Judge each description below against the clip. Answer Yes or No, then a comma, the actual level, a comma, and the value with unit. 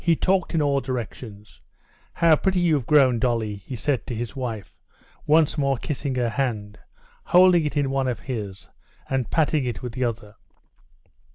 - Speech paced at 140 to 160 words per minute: No, average, 170 wpm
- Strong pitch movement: No, average, 4.6 semitones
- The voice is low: Yes, low, 130 Hz